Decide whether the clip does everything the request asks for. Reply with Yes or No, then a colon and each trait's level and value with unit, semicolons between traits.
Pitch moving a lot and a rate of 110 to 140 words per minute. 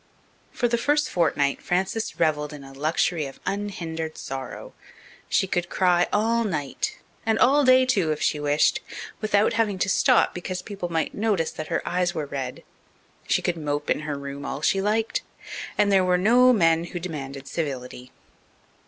No: wide, 5.8 semitones; average, 170 wpm